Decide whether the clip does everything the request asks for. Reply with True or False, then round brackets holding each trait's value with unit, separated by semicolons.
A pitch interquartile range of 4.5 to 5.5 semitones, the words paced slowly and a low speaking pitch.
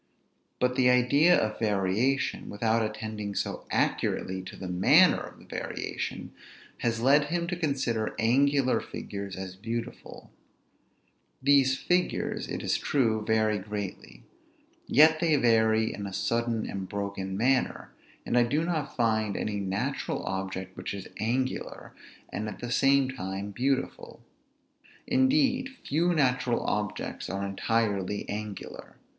True (5.0 semitones; 130 wpm; 115 Hz)